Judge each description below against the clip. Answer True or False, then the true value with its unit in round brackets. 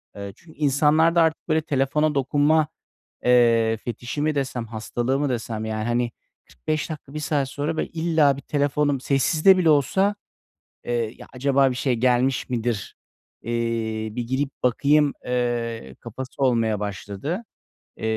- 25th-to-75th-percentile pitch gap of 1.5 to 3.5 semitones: False (4.2 semitones)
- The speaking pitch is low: True (130 Hz)